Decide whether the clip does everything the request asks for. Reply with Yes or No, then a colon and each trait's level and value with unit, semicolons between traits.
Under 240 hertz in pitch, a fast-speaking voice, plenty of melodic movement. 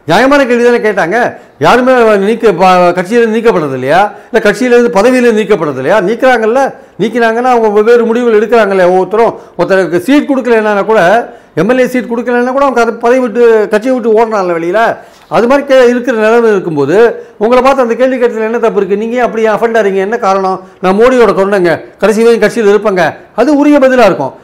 No: high, 230 Hz; fast, 165 wpm; average, 2.9 semitones